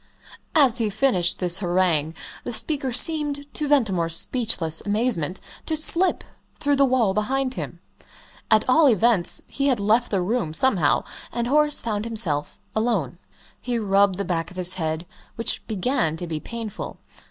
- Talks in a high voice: Yes, high, 215 Hz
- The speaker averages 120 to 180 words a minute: Yes, average, 155 wpm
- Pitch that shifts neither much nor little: No, wide, 6.4 semitones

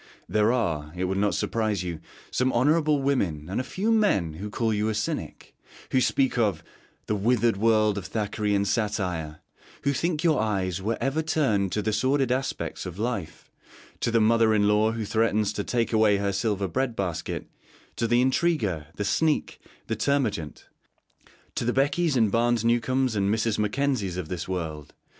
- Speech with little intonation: No, average, 4.3 semitones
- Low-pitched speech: Yes, low, 110 Hz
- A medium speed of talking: Yes, average, 175 wpm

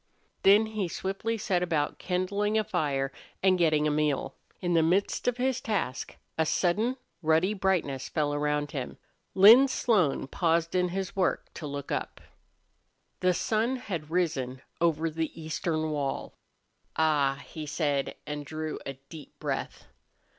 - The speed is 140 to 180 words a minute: Yes, average, 145 wpm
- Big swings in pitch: No, average, 4.5 semitones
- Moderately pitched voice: Yes, medium, 165 Hz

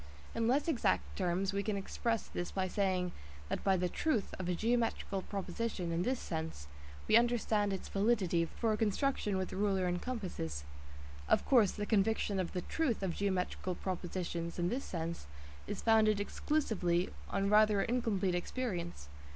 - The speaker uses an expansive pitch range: No, average, 3.9 semitones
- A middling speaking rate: Yes, average, 160 wpm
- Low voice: No, high, 195 Hz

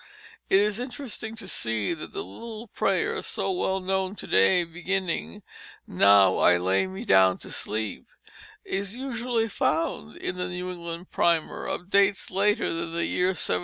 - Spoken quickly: No, average, 165 wpm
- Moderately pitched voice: Yes, medium, 180 Hz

